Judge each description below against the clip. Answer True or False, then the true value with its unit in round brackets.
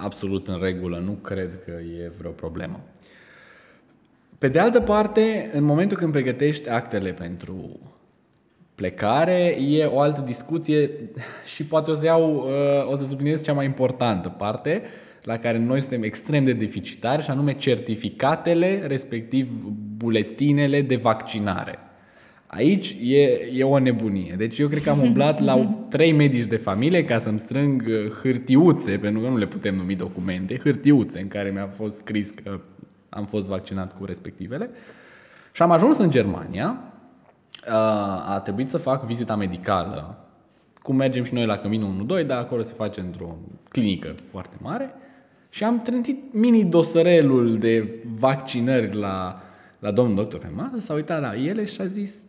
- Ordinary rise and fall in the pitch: False (6.4 semitones)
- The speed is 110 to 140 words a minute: False (150 wpm)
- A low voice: True (120 Hz)